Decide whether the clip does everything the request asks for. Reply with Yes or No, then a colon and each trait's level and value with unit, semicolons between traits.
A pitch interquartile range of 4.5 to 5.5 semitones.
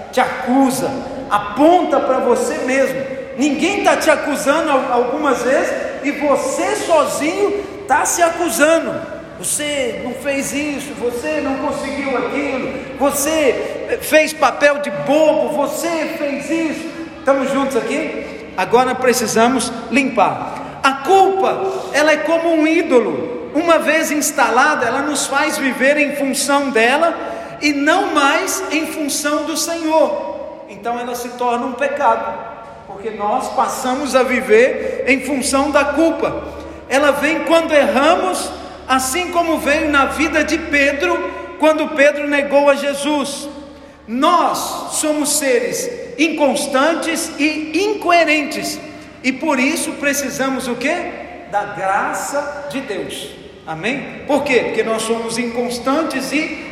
No: average, 2.8 semitones